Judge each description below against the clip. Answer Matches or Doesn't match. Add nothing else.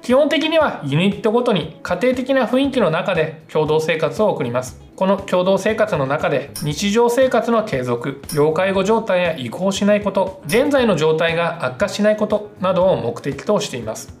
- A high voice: Matches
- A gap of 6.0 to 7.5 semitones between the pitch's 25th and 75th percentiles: Matches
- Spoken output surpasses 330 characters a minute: Matches